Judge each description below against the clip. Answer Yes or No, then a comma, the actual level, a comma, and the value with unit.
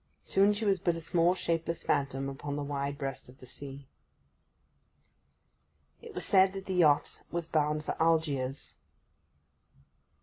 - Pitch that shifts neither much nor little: Yes, average, 4.2 semitones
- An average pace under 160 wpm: Yes, average, 145 wpm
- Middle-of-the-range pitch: Yes, medium, 155 Hz